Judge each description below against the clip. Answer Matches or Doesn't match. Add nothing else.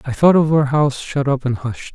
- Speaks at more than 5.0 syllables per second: Matches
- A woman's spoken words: Doesn't match